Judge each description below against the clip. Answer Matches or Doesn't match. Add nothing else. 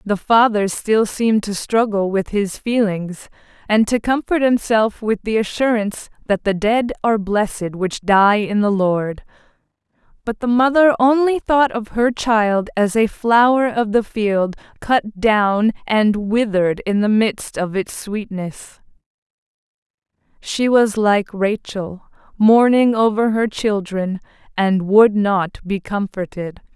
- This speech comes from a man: Doesn't match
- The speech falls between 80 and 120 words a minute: Doesn't match